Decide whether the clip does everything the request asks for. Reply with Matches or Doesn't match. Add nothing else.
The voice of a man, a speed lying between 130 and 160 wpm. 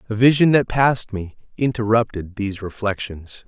Matches